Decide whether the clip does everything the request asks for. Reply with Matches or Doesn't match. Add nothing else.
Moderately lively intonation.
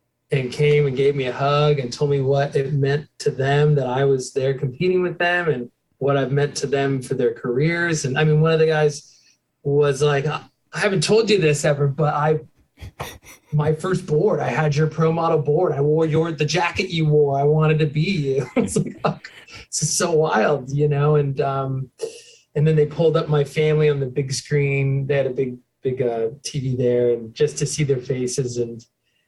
Doesn't match